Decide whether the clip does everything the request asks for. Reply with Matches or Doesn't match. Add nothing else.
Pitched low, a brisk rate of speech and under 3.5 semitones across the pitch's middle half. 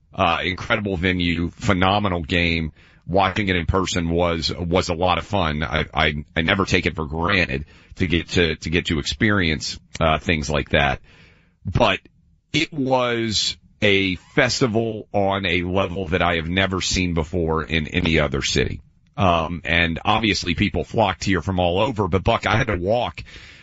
Doesn't match